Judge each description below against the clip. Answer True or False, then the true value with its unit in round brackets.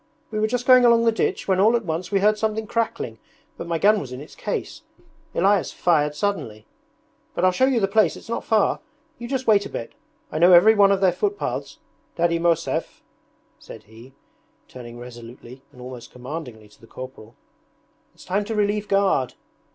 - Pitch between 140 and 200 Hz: True (190 Hz)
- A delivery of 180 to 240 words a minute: True (190 wpm)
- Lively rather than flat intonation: True (8.6 semitones)